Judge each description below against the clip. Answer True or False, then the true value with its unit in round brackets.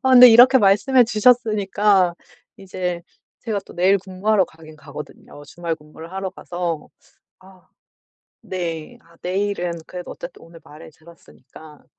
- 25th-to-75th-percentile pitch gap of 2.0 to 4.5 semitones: True (3.7 semitones)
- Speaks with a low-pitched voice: False (185 Hz)